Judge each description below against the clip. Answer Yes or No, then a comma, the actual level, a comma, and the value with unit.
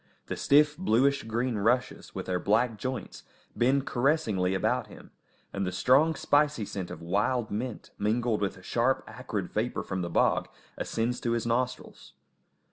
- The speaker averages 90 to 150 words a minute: No, average, 160 wpm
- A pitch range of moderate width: Yes, average, 4.1 semitones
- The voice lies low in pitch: Yes, low, 120 Hz